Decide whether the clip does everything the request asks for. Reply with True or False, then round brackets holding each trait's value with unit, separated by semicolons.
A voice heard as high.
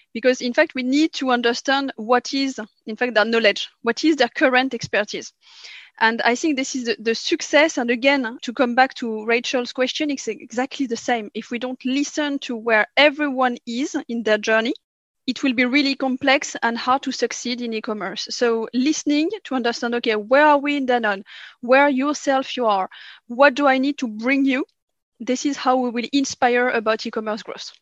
True (255 Hz)